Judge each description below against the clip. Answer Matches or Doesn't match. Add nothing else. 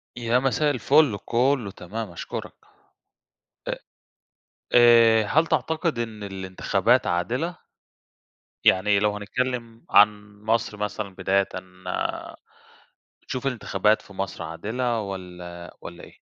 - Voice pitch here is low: Matches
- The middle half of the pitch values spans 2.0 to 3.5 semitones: Doesn't match